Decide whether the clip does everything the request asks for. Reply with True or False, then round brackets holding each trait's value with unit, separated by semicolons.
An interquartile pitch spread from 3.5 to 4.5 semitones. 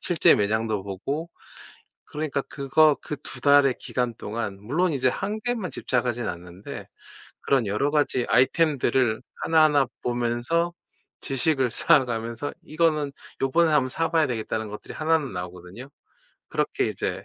False (5.1 semitones)